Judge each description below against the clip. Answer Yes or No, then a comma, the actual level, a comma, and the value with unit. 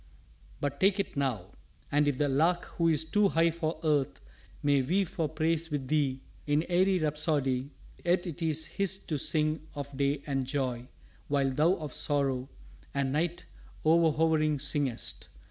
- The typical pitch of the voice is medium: Yes, medium, 150 Hz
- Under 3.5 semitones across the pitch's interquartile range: Yes, average, 3.0 semitones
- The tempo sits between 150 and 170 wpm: Yes, average, 160 wpm